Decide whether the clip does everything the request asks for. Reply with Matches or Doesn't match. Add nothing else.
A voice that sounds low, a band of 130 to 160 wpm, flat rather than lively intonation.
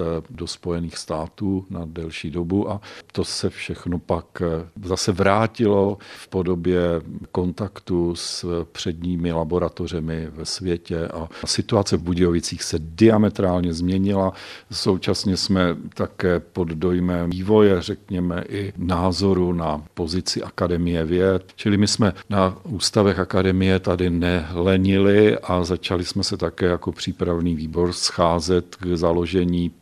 Doesn't match